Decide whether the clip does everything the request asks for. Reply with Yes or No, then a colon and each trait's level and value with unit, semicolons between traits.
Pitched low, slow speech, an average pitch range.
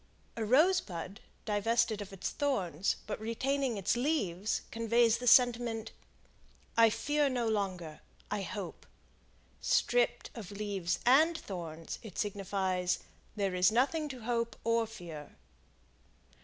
No: high, 220 Hz; slow, 120 wpm; average, 4.2 semitones